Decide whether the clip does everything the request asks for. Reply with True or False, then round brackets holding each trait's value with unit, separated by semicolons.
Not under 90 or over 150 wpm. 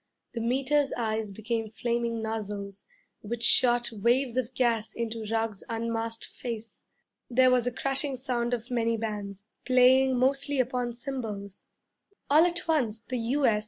True (140 wpm)